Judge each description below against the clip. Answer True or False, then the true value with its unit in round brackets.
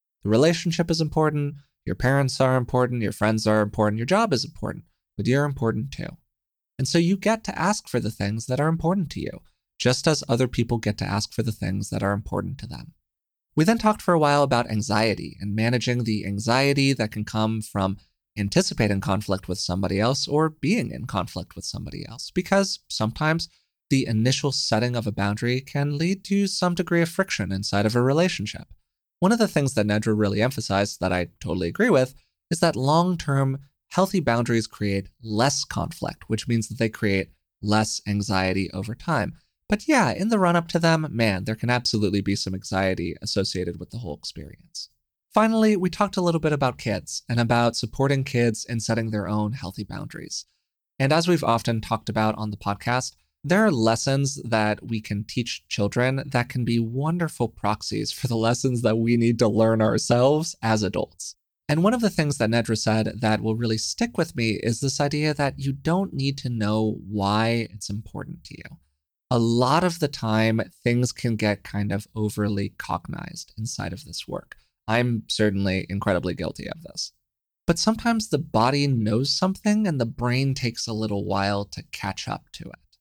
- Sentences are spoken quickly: False (190 wpm)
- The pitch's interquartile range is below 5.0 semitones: False (5.5 semitones)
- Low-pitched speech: True (115 Hz)